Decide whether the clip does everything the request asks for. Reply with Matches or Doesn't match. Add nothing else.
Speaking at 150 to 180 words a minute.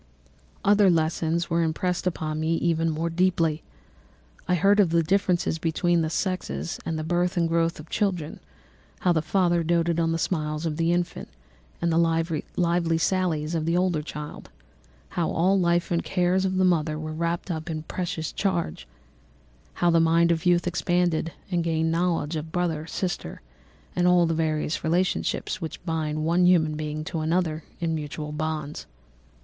Matches